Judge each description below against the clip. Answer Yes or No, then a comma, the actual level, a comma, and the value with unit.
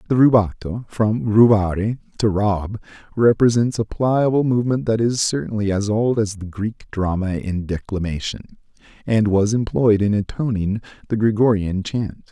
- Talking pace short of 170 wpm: Yes, average, 140 wpm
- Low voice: Yes, low, 105 Hz